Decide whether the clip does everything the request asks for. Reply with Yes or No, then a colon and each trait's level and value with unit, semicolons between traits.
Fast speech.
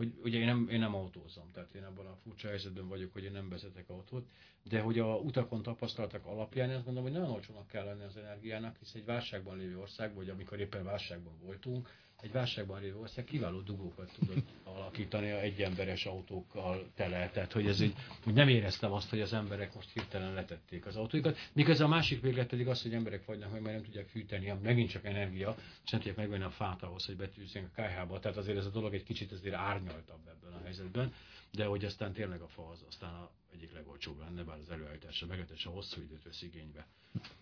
Yes: fast, 215 wpm